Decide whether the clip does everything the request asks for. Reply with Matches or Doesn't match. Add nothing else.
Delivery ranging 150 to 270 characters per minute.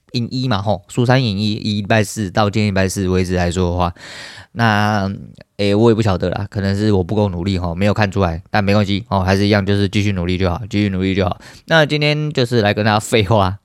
Doesn't match